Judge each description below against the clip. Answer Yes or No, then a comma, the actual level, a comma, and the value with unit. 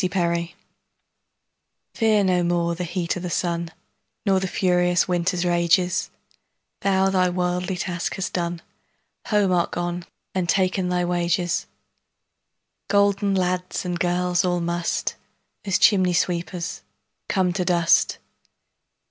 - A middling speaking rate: No, slow, 105 wpm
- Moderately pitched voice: Yes, medium, 180 Hz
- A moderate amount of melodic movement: No, narrow, 1.4 semitones